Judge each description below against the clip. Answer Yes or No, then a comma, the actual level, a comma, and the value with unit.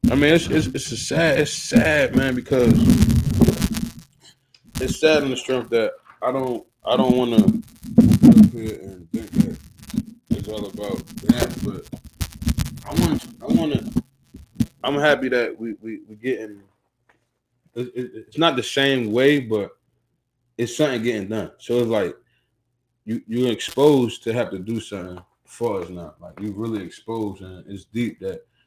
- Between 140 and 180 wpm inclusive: Yes, average, 155 wpm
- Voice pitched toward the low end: Yes, low, 120 Hz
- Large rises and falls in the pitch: No, average, 4.5 semitones